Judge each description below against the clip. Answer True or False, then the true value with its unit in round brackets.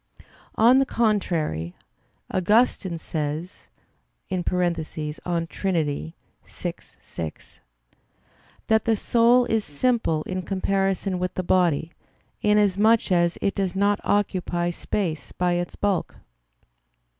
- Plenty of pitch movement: False (3.6 semitones)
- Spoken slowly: True (100 wpm)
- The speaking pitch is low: False (185 Hz)